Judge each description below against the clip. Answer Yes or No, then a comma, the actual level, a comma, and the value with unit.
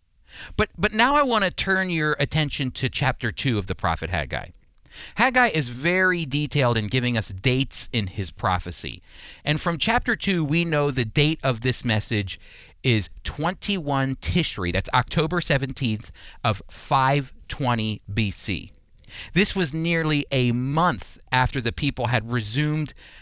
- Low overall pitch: Yes, low, 130 Hz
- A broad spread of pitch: Yes, wide, 6.6 semitones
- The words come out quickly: No, average, 145 wpm